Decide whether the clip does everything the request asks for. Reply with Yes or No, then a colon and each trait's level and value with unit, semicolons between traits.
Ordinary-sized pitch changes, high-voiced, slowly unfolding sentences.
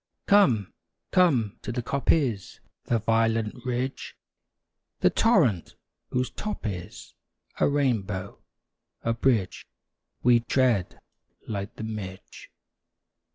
No: average, 4.0 semitones; low, 115 Hz; slow, 100 wpm